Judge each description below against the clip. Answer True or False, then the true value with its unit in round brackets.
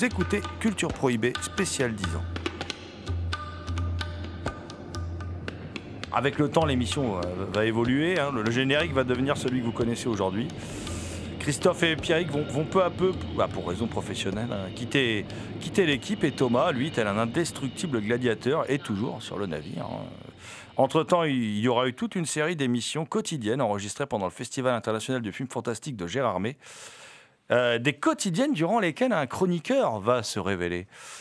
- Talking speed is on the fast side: False (160 wpm)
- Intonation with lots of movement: True (6.7 semitones)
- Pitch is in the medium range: False (125 Hz)